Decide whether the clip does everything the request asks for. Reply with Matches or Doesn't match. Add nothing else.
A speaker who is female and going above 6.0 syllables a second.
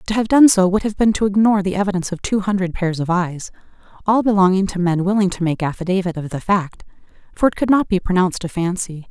Matches